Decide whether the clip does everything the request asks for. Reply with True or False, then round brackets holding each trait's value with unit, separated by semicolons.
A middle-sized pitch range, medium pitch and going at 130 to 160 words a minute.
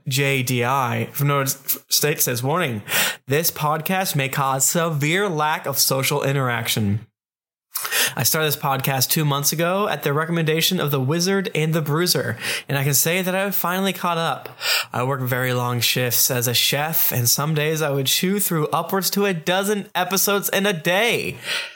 False (4.5 semitones; 150 Hz; 180 wpm)